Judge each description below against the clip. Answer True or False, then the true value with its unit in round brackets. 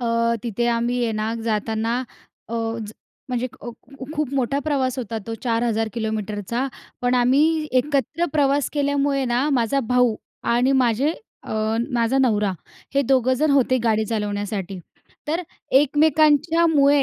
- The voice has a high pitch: True (245 Hz)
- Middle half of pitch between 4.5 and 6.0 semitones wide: False (3.7 semitones)